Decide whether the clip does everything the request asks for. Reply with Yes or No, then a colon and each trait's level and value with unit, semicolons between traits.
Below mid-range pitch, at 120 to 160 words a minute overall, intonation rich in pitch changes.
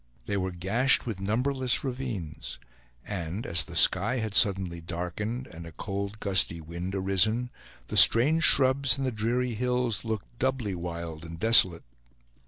Yes: low, 105 Hz; average, 150 wpm; wide, 6.0 semitones